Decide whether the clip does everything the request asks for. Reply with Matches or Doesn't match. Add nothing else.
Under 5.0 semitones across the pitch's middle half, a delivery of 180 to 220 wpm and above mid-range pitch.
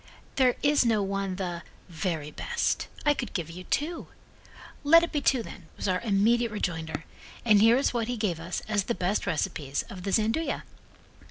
Doesn't match